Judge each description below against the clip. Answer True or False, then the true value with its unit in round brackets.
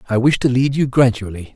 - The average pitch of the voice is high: False (120 Hz)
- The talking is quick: True (230 wpm)